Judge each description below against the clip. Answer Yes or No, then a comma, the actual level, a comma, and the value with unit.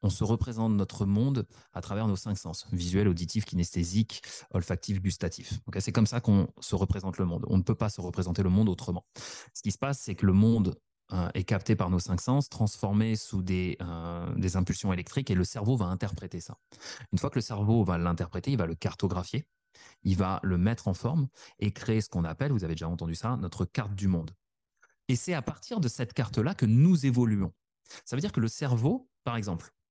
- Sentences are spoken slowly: No, fast, 220 wpm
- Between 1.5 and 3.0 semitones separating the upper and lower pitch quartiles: No, average, 4.2 semitones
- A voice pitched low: Yes, low, 100 Hz